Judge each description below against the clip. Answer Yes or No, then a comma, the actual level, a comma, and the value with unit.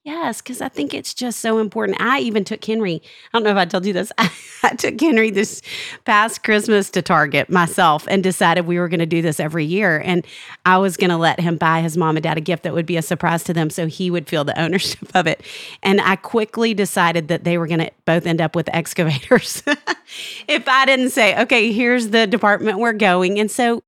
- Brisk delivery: Yes, fast, 240 wpm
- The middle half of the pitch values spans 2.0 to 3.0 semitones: No, average, 4.7 semitones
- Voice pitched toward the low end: No, medium, 185 Hz